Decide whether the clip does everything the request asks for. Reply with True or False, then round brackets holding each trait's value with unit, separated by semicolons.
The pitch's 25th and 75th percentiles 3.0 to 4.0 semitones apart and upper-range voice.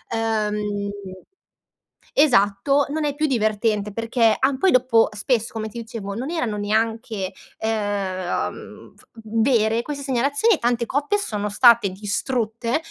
True (3.7 semitones; 225 Hz)